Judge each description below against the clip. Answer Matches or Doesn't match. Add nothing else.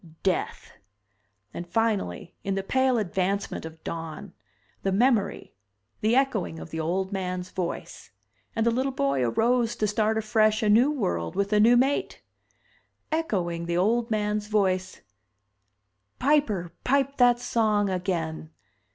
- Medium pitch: Doesn't match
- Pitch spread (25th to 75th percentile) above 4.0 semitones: Matches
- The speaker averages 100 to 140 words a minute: Matches